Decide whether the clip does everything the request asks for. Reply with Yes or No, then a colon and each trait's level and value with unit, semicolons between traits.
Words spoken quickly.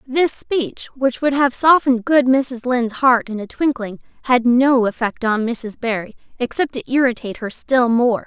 No: average, 180 wpm